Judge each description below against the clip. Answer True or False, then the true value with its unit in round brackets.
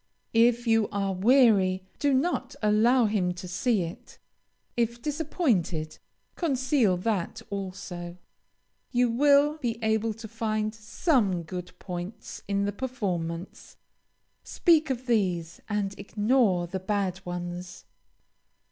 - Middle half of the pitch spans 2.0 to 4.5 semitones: False (4.9 semitones)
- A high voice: True (210 Hz)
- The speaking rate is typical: False (115 wpm)